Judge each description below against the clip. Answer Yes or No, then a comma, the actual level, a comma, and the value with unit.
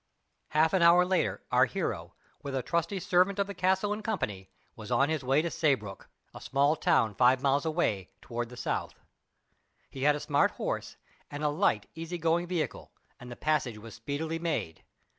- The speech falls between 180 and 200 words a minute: Yes, average, 185 wpm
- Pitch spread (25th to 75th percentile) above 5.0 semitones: Yes, wide, 5.5 semitones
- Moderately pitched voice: Yes, medium, 150 Hz